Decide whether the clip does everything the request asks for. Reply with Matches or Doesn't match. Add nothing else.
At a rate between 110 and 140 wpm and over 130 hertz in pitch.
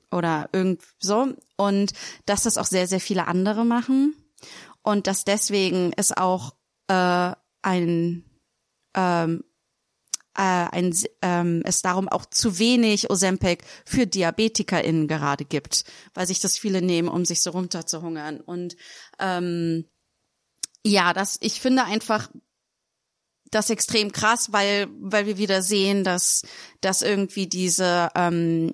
Matches